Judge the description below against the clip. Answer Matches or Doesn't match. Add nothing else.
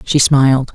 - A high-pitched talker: Doesn't match